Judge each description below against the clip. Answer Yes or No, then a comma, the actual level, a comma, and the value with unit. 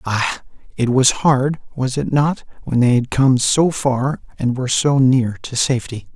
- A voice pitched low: Yes, low, 130 Hz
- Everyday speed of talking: Yes, average, 185 wpm